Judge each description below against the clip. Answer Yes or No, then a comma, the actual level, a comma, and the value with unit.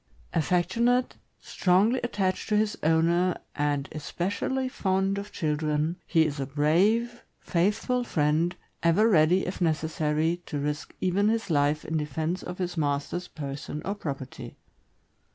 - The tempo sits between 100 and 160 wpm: Yes, slow, 135 wpm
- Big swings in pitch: No, average, 4.7 semitones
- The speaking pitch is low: No, medium, 170 Hz